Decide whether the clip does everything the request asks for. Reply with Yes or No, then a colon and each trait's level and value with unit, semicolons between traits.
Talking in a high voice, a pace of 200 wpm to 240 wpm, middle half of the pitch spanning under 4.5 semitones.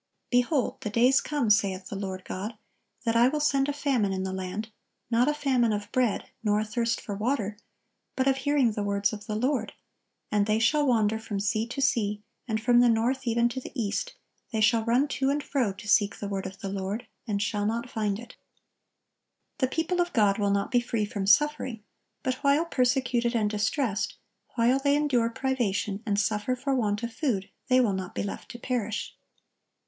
Yes: high, 230 Hz; fast, 205 wpm; average, 3.9 semitones